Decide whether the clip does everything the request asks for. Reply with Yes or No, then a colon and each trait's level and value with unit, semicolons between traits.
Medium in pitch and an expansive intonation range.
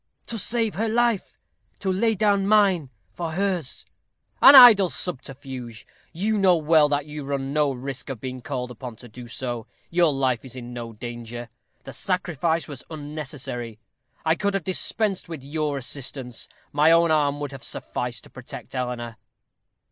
Yes: medium, 145 Hz; wide, 6.2 semitones